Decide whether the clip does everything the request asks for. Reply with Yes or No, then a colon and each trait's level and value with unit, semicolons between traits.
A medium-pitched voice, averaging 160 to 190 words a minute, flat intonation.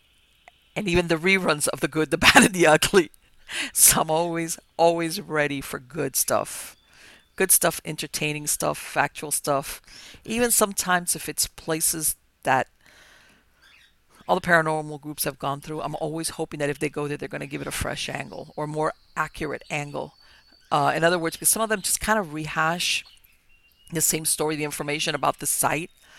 Yes: medium, 155 Hz; average, 180 wpm; narrow, 2.0 semitones